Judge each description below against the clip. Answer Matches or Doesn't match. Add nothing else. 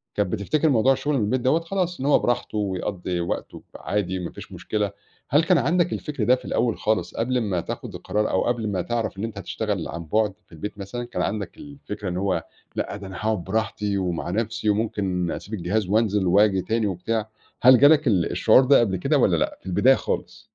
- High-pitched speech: Doesn't match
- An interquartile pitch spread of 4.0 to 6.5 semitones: Matches